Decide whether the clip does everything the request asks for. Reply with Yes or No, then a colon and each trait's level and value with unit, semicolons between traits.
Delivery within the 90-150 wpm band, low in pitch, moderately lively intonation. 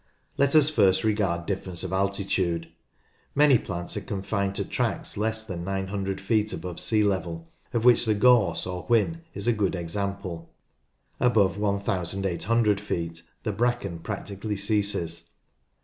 Yes: average, 140 wpm; low, 100 Hz; average, 3.1 semitones